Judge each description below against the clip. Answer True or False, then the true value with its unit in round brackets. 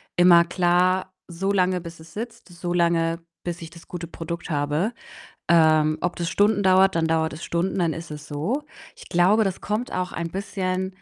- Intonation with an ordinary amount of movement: False (2.2 semitones)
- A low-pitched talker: False (175 Hz)